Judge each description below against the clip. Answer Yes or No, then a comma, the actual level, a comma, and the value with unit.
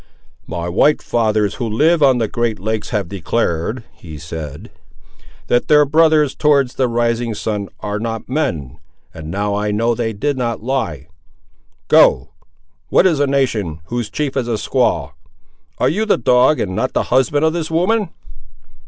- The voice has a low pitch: Yes, low, 115 Hz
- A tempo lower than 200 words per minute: Yes, average, 160 wpm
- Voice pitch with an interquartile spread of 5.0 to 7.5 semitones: Yes, average, 5.3 semitones